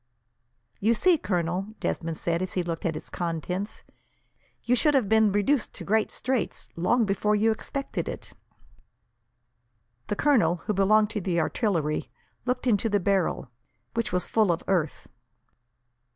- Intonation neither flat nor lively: Yes, average, 4.3 semitones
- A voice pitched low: No, high, 200 Hz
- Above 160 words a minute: No, average, 150 wpm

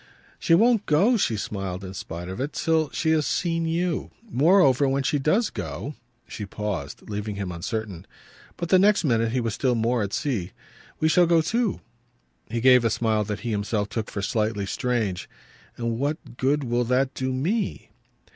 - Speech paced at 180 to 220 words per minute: Yes, average, 185 wpm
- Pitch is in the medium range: No, low, 125 Hz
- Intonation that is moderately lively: No, wide, 7.0 semitones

